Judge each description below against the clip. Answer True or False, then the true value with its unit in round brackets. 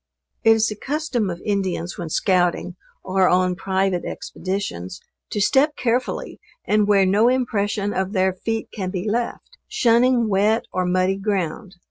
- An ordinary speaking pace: True (150 wpm)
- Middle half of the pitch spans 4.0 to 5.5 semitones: False (3.3 semitones)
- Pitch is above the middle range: True (200 Hz)